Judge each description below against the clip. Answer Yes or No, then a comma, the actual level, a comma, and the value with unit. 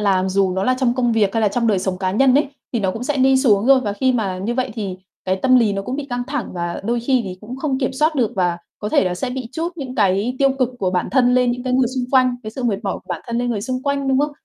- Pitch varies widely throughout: No, average, 4.7 semitones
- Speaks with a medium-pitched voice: No, high, 240 Hz